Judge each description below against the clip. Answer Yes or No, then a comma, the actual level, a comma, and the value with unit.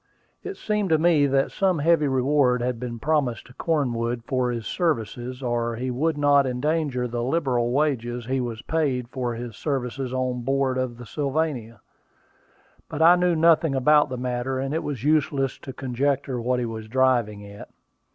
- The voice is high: No, low, 130 Hz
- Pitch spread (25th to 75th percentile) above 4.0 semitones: No, average, 3.4 semitones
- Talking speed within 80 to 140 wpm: No, average, 175 wpm